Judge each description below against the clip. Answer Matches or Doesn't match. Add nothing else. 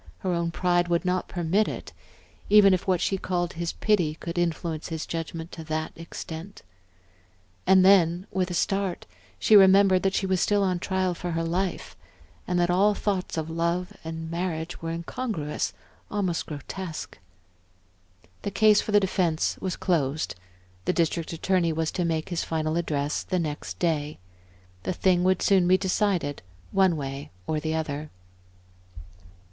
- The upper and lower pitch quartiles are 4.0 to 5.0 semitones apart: Doesn't match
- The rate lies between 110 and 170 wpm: Matches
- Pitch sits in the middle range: Matches